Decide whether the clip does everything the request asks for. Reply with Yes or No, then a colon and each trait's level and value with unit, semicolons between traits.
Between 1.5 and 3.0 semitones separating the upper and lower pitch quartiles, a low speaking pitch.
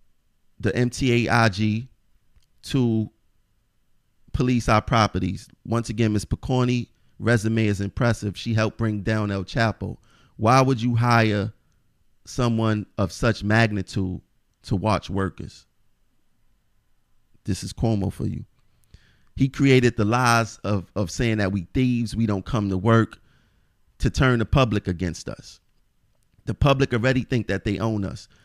Yes: average, 2.7 semitones; low, 110 Hz